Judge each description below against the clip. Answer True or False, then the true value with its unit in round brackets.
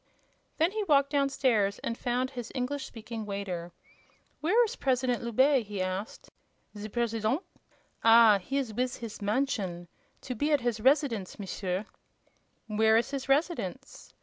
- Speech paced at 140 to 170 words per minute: True (145 wpm)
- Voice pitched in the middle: False (235 Hz)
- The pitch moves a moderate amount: True (4.5 semitones)